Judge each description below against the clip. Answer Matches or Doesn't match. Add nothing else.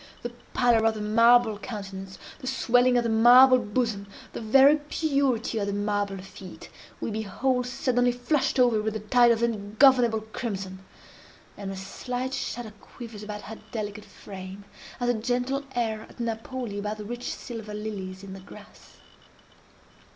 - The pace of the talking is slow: Doesn't match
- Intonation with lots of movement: Doesn't match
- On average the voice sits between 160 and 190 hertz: Doesn't match